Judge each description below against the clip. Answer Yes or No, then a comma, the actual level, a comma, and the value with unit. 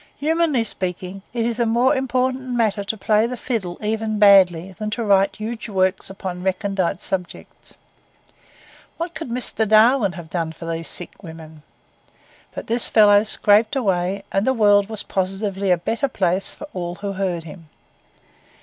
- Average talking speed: Yes, average, 160 wpm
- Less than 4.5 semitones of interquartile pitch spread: Yes, average, 3.7 semitones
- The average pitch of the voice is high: Yes, high, 205 Hz